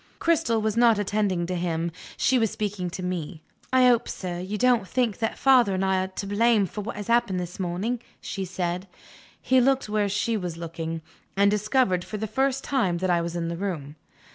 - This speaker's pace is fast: Yes, fast, 210 wpm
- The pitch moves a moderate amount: Yes, average, 4.5 semitones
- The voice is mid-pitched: No, high, 200 Hz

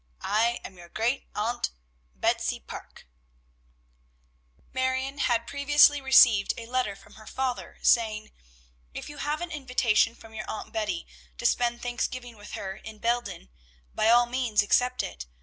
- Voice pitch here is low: No, high, 240 Hz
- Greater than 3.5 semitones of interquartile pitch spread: No, average, 3.2 semitones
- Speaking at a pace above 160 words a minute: No, average, 150 wpm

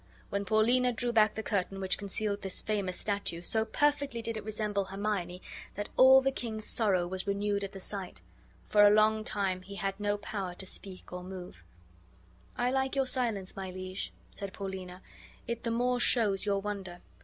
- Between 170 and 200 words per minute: Yes, average, 185 wpm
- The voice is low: No, high, 205 Hz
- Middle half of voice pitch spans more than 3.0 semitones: No, narrow, 2.6 semitones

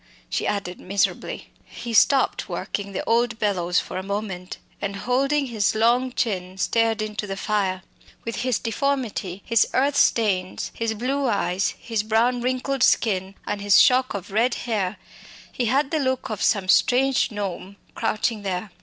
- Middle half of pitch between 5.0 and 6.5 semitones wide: No, average, 3.9 semitones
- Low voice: No, high, 220 Hz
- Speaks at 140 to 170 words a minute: Yes, average, 160 wpm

